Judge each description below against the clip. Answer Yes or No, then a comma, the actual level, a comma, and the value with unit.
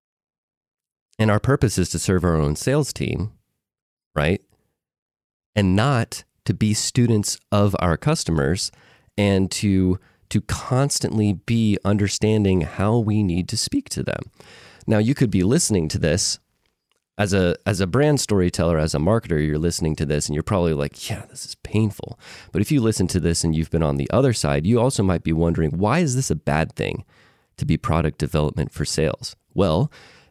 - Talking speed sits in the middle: Yes, average, 180 wpm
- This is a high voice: No, low, 100 Hz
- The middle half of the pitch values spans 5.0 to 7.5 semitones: Yes, average, 5.3 semitones